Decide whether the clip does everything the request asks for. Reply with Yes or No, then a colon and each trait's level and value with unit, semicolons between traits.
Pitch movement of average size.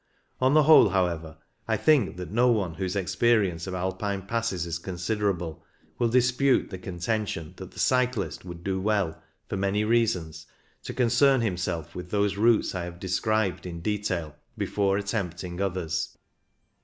Yes: average, 4.0 semitones